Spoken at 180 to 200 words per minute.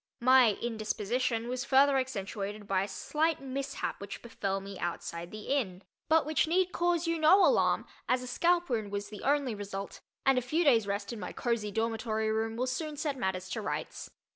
Yes: average, 190 wpm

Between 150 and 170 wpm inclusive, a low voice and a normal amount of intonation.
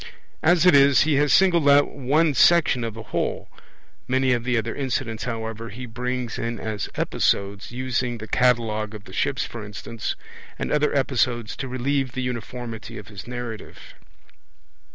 Yes: average, 165 wpm; low, 125 Hz; average, 3.3 semitones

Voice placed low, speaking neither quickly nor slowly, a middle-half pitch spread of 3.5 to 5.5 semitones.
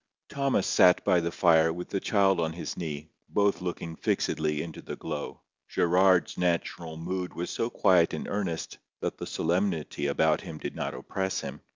No: very low, 85 Hz; average, 175 wpm; average, 2.7 semitones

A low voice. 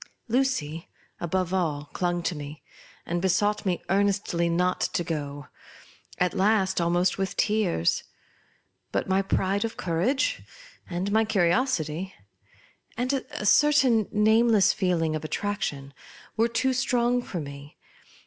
No: high, 190 Hz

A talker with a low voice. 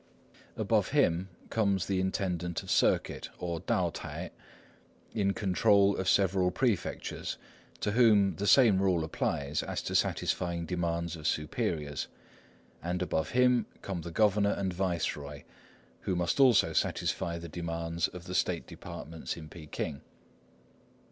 Yes: very low, 90 Hz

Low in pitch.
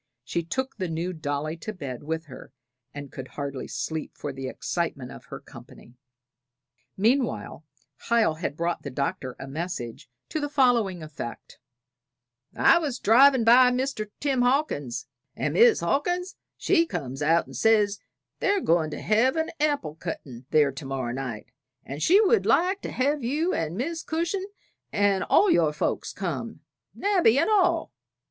No: medium, 185 Hz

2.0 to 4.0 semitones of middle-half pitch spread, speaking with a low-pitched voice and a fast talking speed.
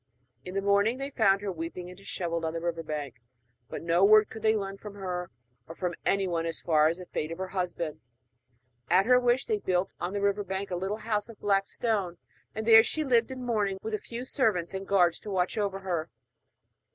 No: average, 3.5 semitones; high, 195 Hz; fast, 220 wpm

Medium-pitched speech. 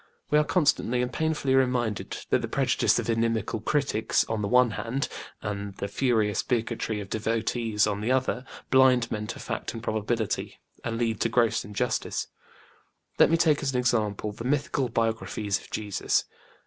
No: low, 115 Hz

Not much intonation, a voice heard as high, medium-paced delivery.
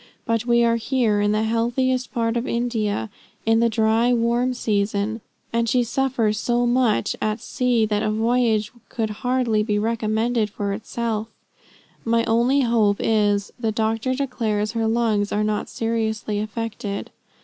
Yes: narrow, 2.0 semitones; high, 225 Hz; average, 150 wpm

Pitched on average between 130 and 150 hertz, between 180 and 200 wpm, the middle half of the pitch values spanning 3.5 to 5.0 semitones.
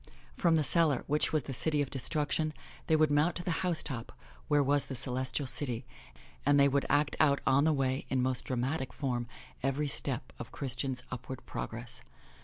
No: medium, 140 Hz; average, 185 wpm; narrow, 2.6 semitones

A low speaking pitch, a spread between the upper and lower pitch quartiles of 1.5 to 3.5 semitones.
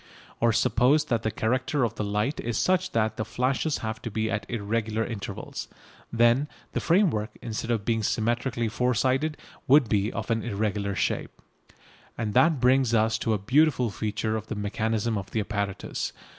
Yes: low, 115 Hz; average, 2.7 semitones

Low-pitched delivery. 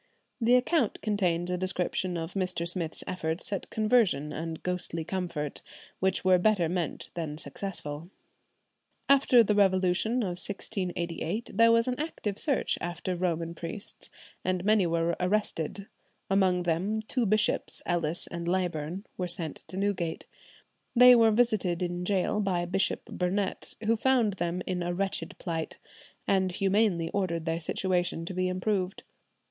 No: medium, 185 Hz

